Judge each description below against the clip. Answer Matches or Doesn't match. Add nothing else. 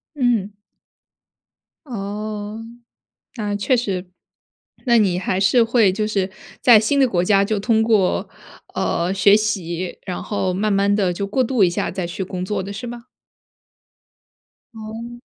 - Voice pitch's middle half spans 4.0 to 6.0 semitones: Doesn't match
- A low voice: Doesn't match